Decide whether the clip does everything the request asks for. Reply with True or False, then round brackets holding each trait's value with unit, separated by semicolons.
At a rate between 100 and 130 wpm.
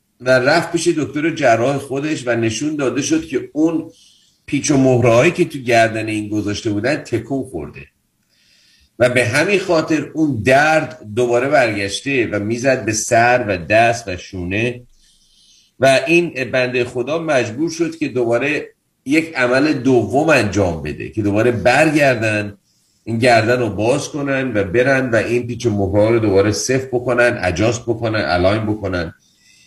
False (150 wpm)